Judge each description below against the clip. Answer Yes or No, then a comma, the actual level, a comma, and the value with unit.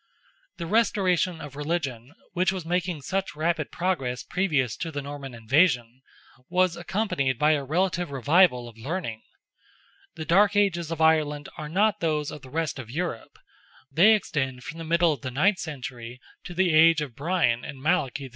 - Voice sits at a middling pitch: Yes, medium, 155 Hz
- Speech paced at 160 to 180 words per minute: Yes, average, 170 wpm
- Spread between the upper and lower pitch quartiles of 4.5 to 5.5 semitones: Yes, average, 4.9 semitones